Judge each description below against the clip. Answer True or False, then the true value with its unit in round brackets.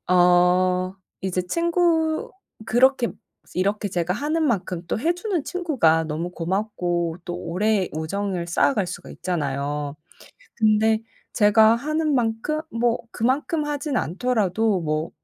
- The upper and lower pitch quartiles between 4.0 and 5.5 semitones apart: False (6.9 semitones)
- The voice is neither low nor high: False (205 Hz)